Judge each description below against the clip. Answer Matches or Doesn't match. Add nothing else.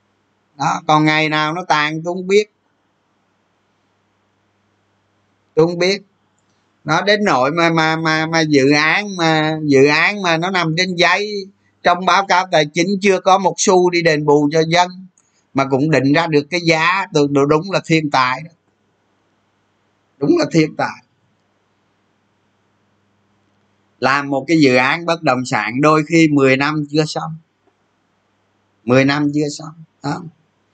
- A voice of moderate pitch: Matches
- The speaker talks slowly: Matches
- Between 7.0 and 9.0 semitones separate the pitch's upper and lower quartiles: Matches